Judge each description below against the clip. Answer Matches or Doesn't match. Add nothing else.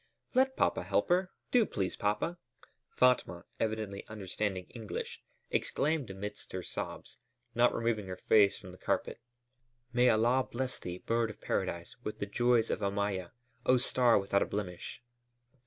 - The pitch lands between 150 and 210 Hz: Doesn't match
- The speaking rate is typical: Matches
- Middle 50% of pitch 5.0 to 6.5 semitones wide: Doesn't match